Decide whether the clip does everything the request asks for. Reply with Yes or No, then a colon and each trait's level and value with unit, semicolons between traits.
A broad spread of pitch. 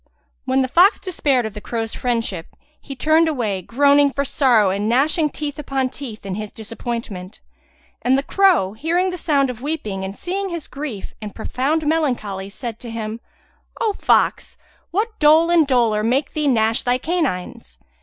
Yes: wide, 5.8 semitones